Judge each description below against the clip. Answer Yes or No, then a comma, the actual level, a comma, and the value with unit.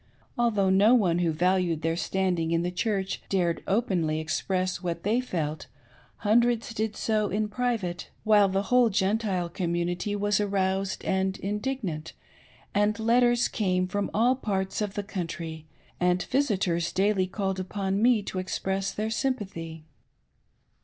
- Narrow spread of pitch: No, average, 3.2 semitones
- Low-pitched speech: No, high, 195 Hz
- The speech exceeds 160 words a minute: No, average, 145 wpm